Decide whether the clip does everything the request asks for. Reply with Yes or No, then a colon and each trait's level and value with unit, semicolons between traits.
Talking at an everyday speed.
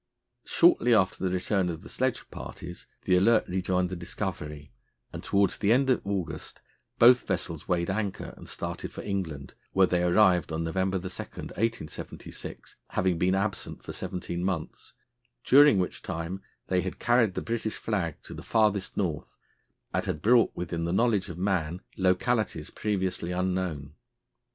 Yes: average, 155 wpm